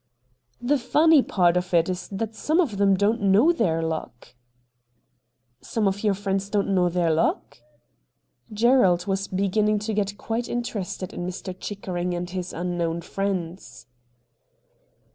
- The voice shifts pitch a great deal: No, average, 3.3 semitones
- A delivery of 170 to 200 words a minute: No, average, 160 wpm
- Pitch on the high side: Yes, high, 195 Hz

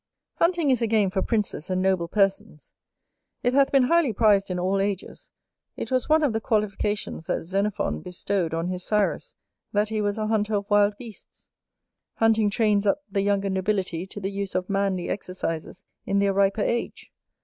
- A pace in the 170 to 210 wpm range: Yes, average, 180 wpm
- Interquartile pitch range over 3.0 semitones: No, narrow, 2.4 semitones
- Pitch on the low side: No, high, 200 Hz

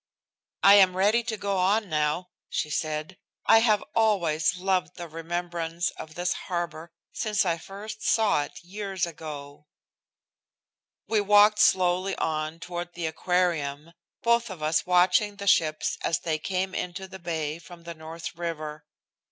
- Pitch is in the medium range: Yes, medium, 175 Hz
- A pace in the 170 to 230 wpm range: No, average, 150 wpm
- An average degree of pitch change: Yes, average, 3.5 semitones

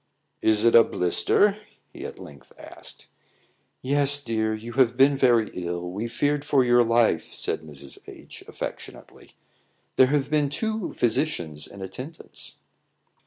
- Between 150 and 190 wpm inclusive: No, average, 140 wpm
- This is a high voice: No, low, 120 Hz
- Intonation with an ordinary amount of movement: No, wide, 6.1 semitones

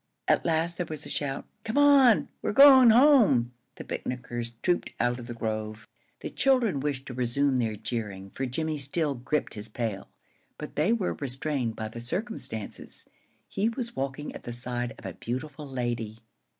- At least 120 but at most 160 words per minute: No, average, 175 wpm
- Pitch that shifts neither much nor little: No, wide, 6.6 semitones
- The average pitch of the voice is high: No, low, 135 Hz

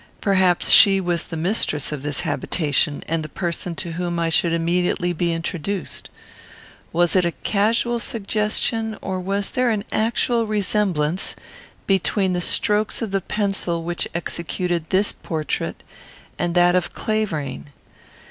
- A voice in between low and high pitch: Yes, medium, 180 Hz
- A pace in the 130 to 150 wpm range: Yes, average, 140 wpm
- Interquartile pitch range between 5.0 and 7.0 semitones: No, average, 3.4 semitones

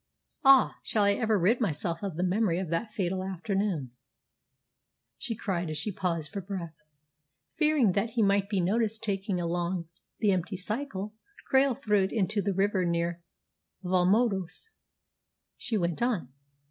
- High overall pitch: Yes, high, 195 Hz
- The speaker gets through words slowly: No, average, 150 wpm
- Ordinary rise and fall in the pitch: Yes, average, 3.6 semitones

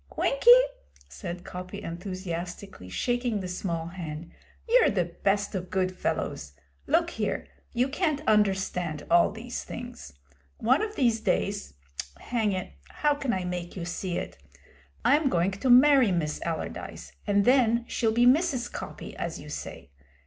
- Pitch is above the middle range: Yes, high, 200 Hz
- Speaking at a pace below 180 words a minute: Yes, average, 150 wpm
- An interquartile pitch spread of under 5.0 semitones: No, wide, 5.6 semitones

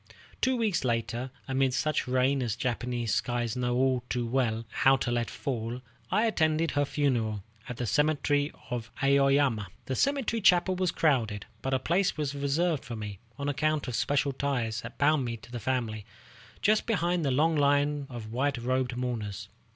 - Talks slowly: No, average, 175 wpm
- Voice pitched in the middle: No, low, 130 Hz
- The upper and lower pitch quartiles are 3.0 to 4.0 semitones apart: Yes, average, 3.6 semitones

